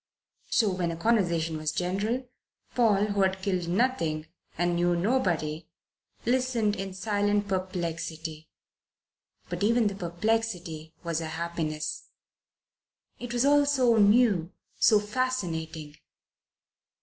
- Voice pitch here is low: No, high, 190 Hz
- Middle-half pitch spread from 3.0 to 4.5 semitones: No, average, 5.2 semitones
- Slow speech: Yes, slow, 110 wpm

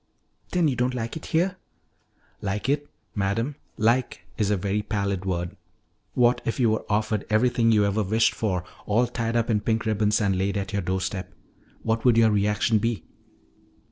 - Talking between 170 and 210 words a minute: Yes, average, 180 wpm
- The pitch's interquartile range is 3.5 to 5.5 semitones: No, average, 2.7 semitones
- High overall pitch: No, low, 110 Hz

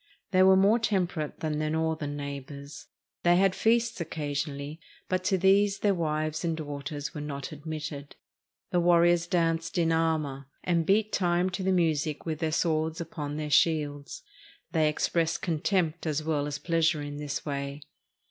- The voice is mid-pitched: Yes, medium, 160 Hz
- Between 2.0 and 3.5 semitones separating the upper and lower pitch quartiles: Yes, average, 2.9 semitones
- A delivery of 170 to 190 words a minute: No, average, 160 wpm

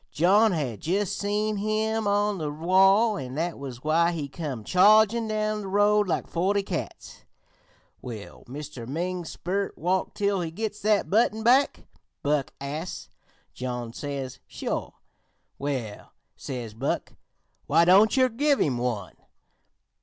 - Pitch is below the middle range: No, medium, 180 Hz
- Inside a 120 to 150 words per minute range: Yes, average, 140 wpm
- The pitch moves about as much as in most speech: No, wide, 6.8 semitones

